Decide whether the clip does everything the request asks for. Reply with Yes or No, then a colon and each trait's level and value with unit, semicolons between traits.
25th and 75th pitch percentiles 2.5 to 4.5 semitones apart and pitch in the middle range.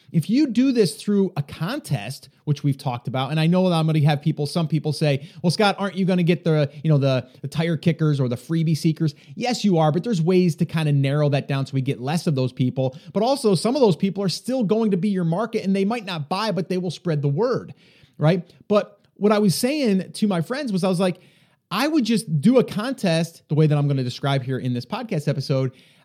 No: average, 5.2 semitones; medium, 165 Hz